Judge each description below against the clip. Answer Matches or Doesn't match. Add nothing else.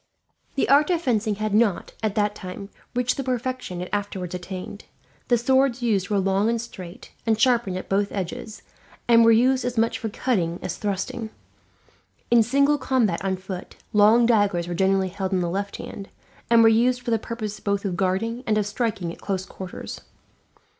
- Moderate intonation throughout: Matches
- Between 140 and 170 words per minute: Doesn't match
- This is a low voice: Doesn't match